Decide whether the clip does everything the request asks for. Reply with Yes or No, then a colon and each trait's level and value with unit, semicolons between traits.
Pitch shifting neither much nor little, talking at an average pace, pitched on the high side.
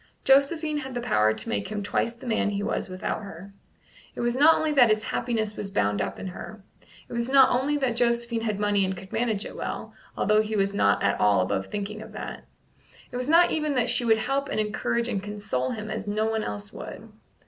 No: average, 3.8 semitones; fast, 230 wpm; high, 215 Hz